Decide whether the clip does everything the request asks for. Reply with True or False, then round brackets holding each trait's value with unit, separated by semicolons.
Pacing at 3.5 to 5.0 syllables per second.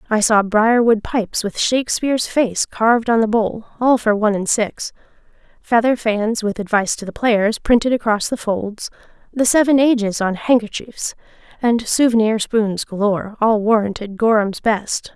True (4.8 syllables/s)